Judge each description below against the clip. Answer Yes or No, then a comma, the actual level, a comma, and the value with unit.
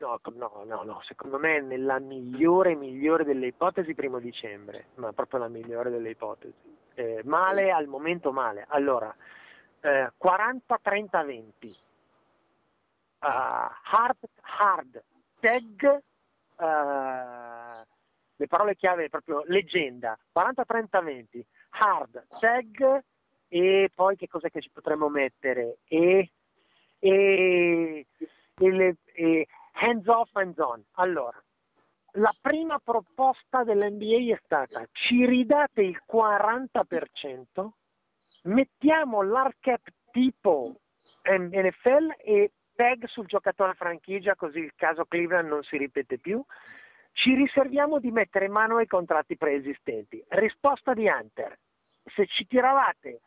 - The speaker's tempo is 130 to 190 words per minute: No, slow, 115 wpm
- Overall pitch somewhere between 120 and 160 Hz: No, high, 190 Hz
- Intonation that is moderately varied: No, wide, 7.5 semitones